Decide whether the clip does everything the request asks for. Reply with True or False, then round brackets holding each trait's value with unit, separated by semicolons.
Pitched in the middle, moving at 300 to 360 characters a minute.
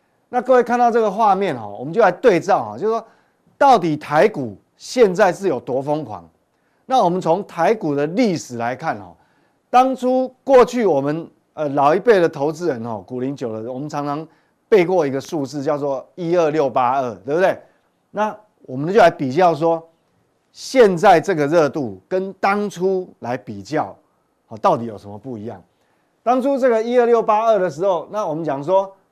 False (170 Hz; 265 characters per minute)